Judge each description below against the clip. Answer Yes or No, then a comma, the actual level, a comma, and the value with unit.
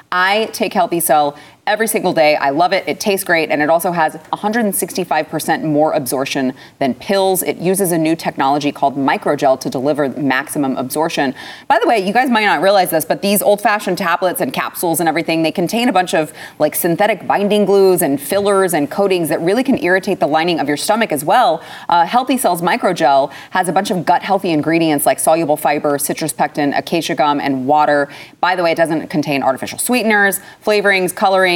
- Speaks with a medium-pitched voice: Yes, medium, 175 Hz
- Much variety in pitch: No, average, 4.3 semitones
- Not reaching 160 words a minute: No, average, 195 wpm